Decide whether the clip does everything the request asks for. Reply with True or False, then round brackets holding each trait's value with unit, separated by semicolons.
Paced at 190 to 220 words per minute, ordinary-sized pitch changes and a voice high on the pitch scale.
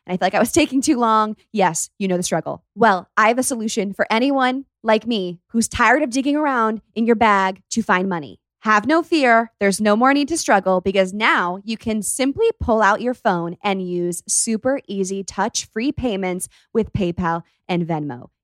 True (205 wpm; 4.2 semitones; 215 Hz)